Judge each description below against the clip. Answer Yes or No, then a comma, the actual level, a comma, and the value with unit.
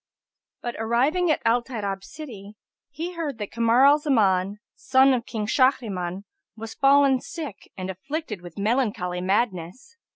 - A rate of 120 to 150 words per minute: Yes, average, 140 wpm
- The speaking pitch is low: No, high, 235 Hz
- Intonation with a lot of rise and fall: Yes, wide, 5.7 semitones